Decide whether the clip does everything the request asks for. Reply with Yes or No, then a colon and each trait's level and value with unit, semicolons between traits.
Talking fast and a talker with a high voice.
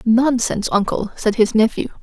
No: average, 150 wpm; high, 225 Hz